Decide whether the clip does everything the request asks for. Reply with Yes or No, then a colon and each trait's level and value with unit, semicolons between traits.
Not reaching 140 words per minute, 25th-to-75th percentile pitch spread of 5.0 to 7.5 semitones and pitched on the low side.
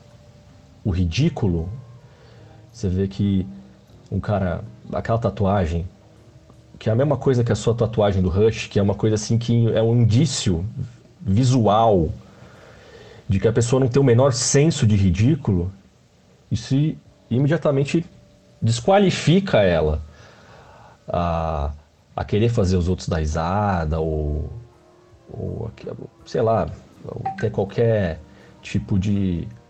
No: average, 125 wpm; average, 4.0 semitones; low, 110 Hz